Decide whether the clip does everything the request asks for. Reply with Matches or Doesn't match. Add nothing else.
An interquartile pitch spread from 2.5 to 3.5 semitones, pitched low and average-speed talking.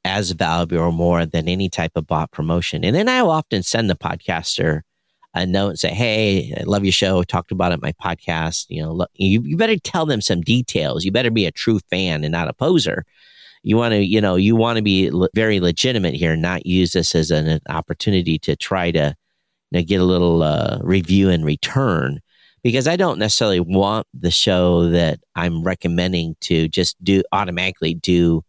Doesn't match